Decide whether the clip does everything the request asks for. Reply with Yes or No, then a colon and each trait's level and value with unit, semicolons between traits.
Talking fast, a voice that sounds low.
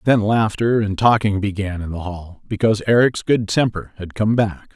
No: average, 190 wpm; low, 105 Hz